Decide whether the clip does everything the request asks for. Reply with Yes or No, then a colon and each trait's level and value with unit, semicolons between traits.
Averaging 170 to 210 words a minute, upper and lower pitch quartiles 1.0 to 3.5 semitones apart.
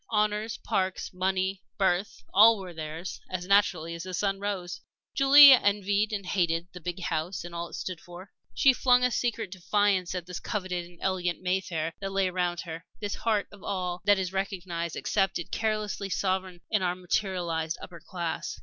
Yes: average, 175 wpm; narrow, 2.5 semitones